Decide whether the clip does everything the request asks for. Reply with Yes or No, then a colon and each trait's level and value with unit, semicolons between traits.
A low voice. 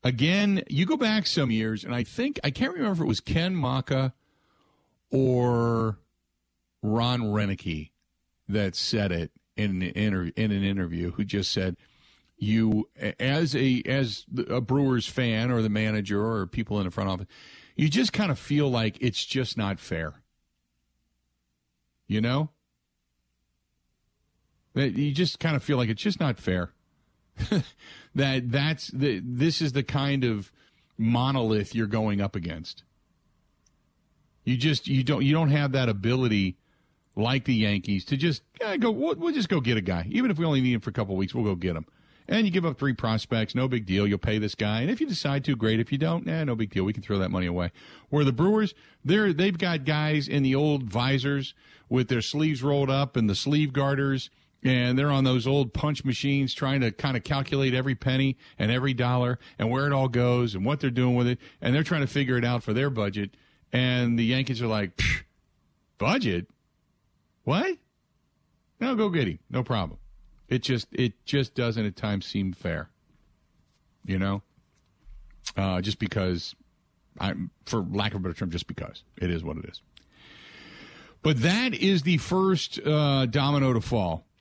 Yes: low, 125 Hz